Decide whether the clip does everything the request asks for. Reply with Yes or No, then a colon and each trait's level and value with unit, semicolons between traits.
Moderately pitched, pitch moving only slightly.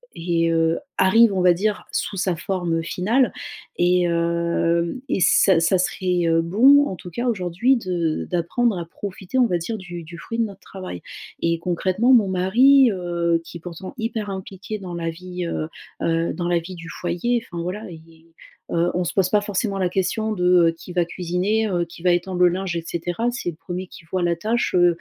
No: medium, 180 Hz; average, 3.0 semitones